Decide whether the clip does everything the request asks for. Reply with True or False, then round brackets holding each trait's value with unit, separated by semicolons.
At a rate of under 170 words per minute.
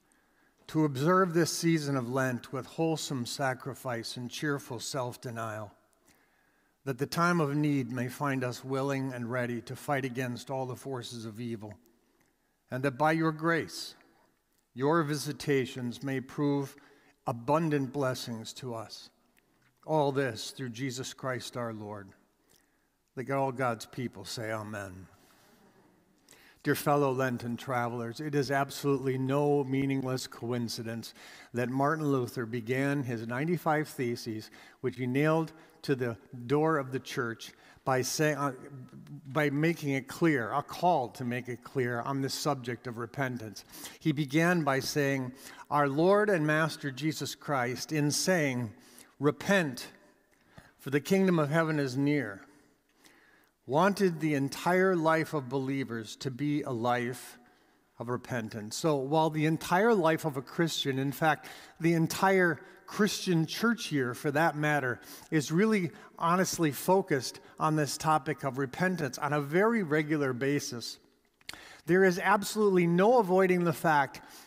True (140 wpm)